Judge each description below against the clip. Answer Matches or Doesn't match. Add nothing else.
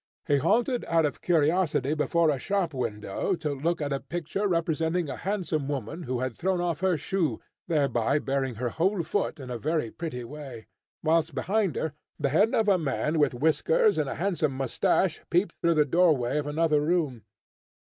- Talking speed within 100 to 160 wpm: Doesn't match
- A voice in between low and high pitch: Matches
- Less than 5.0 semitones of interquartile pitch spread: Matches